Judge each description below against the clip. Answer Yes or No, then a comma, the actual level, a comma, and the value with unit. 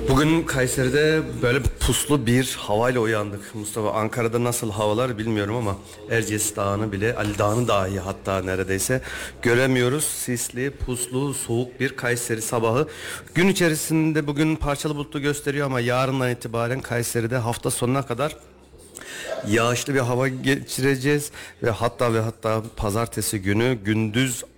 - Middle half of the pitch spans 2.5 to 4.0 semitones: Yes, average, 3.5 semitones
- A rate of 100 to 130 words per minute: Yes, average, 125 wpm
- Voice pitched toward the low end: Yes, low, 120 Hz